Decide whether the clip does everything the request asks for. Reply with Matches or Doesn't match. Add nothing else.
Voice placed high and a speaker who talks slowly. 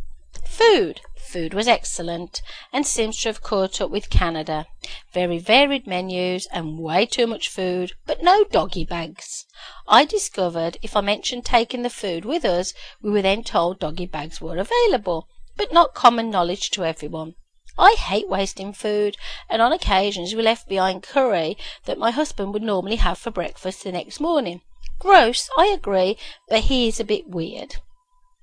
Doesn't match